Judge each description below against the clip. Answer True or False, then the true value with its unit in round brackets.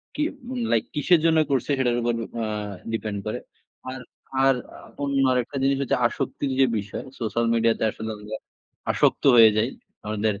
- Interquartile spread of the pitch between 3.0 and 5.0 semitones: True (3.9 semitones)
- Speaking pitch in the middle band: False (120 Hz)